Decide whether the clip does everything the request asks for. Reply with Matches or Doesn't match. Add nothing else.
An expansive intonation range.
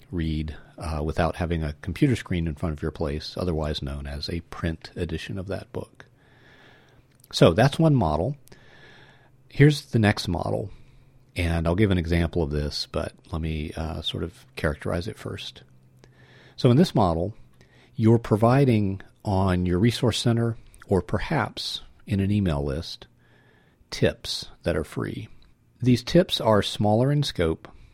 Matches